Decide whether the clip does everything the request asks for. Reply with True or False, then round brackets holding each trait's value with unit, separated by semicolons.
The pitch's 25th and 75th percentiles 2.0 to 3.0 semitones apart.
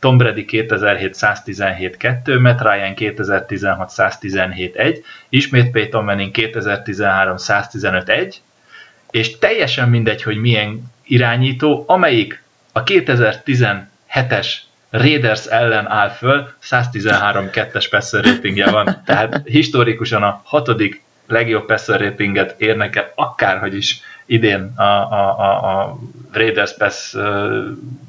False (3.4 semitones)